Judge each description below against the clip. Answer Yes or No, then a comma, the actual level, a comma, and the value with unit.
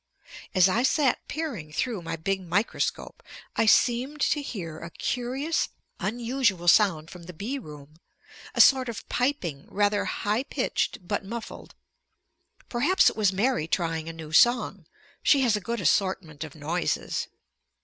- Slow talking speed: No, average, 150 wpm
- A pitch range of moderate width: No, wide, 6.7 semitones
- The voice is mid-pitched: No, high, 205 Hz